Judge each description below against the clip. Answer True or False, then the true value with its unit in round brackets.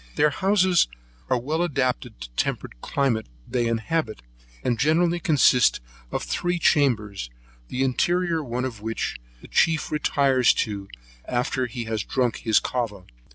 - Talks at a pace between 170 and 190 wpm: False (145 wpm)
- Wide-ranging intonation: True (5.7 semitones)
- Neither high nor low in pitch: False (130 Hz)